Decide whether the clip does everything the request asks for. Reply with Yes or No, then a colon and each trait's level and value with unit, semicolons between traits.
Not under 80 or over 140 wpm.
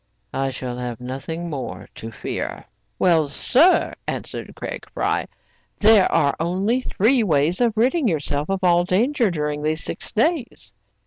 No: average, 150 wpm